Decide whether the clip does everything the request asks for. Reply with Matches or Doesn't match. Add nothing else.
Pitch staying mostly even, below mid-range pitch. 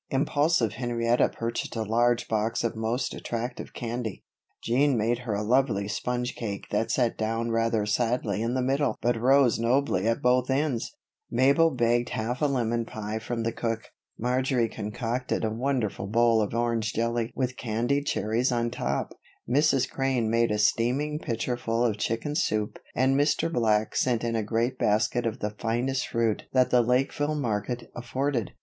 Matches